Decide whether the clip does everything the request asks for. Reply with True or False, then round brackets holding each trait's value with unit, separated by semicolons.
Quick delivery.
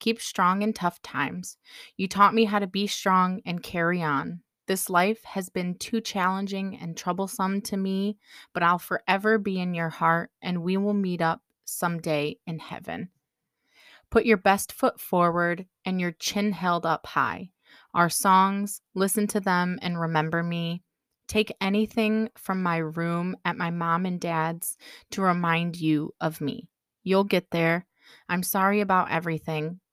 False (160 wpm)